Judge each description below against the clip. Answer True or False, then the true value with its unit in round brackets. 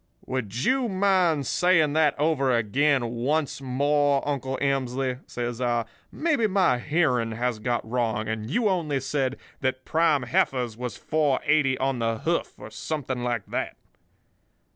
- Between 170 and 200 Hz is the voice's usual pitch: False (135 Hz)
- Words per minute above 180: False (140 wpm)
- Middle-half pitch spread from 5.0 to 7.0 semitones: False (4.0 semitones)